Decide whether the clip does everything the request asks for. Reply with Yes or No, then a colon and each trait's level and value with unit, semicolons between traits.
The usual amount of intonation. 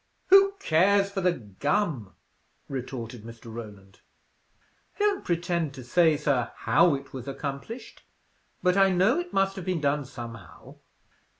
No: wide, 7.8 semitones